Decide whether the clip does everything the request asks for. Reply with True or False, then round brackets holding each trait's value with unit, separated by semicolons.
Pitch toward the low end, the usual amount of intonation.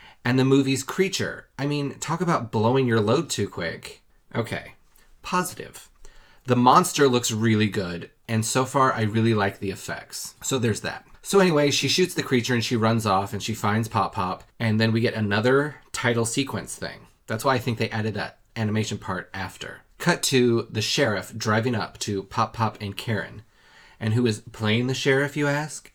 True (115 Hz; 3.8 semitones)